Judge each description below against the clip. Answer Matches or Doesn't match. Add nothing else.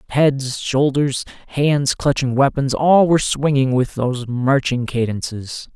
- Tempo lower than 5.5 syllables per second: Matches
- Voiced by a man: Matches